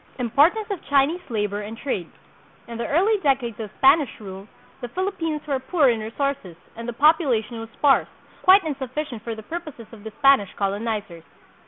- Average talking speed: Yes, average, 170 wpm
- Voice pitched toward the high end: Yes, very high, 255 Hz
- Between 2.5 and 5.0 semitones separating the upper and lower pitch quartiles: No, wide, 5.4 semitones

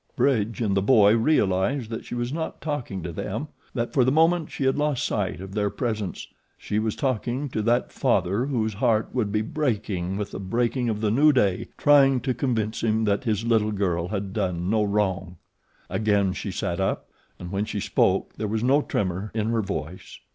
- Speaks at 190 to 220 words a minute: Yes, average, 200 wpm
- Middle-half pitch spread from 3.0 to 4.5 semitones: Yes, average, 3.9 semitones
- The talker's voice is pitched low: Yes, low, 110 Hz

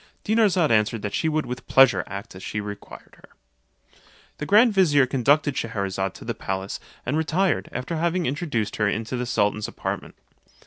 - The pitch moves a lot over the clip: Yes, wide, 7.2 semitones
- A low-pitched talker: Yes, low, 125 Hz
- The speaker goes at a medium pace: Yes, average, 170 wpm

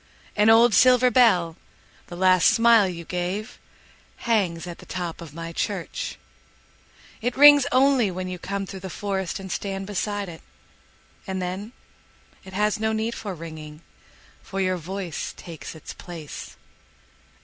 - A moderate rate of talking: No, slow, 130 wpm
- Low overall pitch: No, high, 190 Hz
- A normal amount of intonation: Yes, average, 3.9 semitones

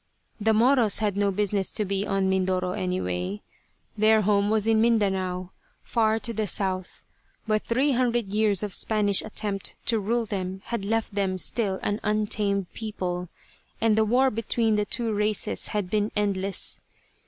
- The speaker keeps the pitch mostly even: Yes, narrow, 2.3 semitones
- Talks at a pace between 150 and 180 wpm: Yes, average, 160 wpm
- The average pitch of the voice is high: Yes, high, 210 Hz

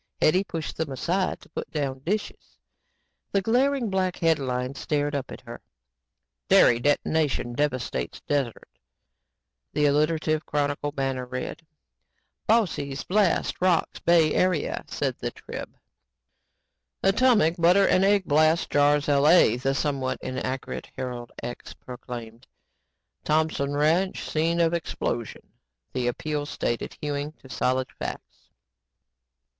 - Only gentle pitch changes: No, average, 4.3 semitones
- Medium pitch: Yes, medium, 150 Hz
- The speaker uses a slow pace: Yes, slow, 120 wpm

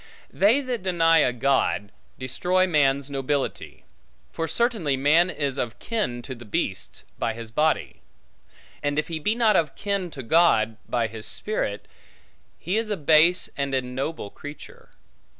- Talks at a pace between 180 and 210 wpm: No, average, 150 wpm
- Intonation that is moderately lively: No, wide, 5.7 semitones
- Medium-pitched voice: Yes, medium, 150 Hz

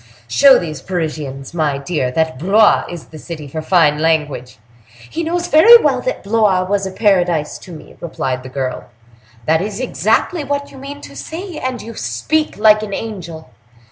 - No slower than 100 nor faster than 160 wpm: No, average, 175 wpm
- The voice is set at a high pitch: No, medium, 180 Hz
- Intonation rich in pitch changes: Yes, wide, 7.2 semitones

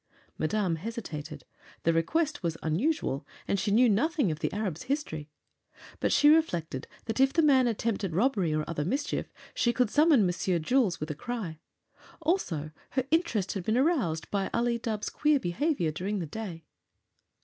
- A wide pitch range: Yes, wide, 8.3 semitones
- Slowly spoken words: No, average, 165 wpm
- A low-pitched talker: No, high, 210 Hz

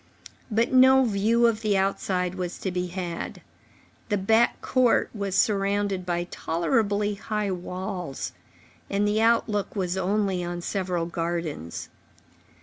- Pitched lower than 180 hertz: No, high, 195 Hz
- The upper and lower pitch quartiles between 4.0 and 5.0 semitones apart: No, average, 3.0 semitones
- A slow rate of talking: Yes, slow, 130 wpm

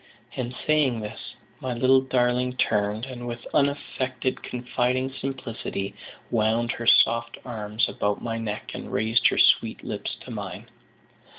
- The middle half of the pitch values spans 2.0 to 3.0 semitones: Yes, narrow, 2.4 semitones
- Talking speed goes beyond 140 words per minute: No, slow, 135 wpm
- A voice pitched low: Yes, low, 120 Hz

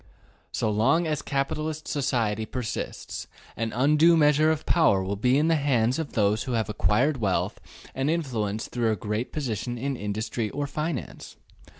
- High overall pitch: No, low, 125 Hz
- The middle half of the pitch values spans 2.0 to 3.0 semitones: No, wide, 5.5 semitones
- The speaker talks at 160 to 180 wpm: Yes, average, 165 wpm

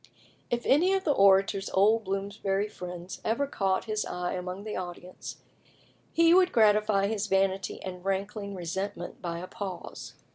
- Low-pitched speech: No, high, 195 Hz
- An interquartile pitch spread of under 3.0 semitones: Yes, narrow, 2.4 semitones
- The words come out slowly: No, average, 150 wpm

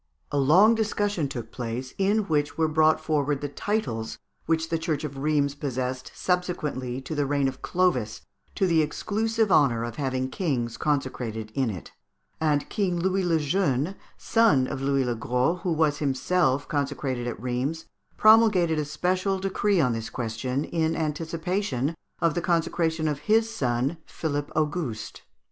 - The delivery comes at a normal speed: Yes, average, 160 wpm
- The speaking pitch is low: No, medium, 150 Hz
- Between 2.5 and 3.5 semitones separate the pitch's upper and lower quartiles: No, average, 5.1 semitones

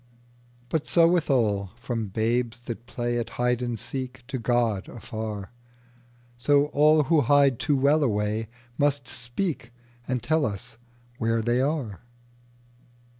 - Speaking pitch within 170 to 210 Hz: No, low, 120 Hz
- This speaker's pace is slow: Yes, slow, 125 wpm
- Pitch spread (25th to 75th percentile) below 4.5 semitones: Yes, average, 3.3 semitones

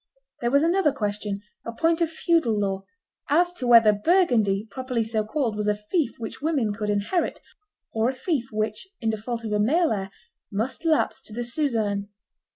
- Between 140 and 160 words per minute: No, average, 180 wpm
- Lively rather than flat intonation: Yes, wide, 6.0 semitones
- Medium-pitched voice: No, high, 230 Hz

